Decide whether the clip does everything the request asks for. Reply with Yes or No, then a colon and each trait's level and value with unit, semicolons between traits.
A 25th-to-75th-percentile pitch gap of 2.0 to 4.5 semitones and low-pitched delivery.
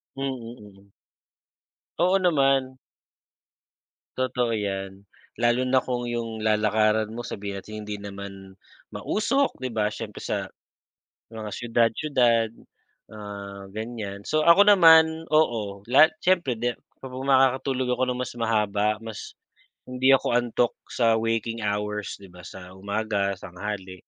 Yes: average, 4.0 semitones; low, 115 Hz